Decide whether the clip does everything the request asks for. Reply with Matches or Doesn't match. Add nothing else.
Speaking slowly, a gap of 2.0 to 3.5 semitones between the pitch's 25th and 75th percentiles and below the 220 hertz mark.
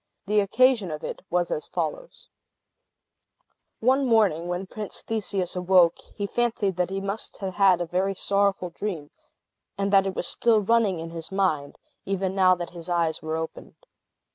Doesn't match